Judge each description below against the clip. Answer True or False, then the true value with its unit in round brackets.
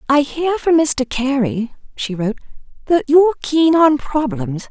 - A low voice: False (275 Hz)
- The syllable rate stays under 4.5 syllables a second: True (4.2 syllables/s)